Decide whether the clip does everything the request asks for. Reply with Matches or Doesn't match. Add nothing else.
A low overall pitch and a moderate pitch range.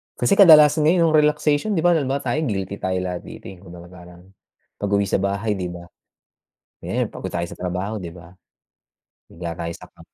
Doesn't match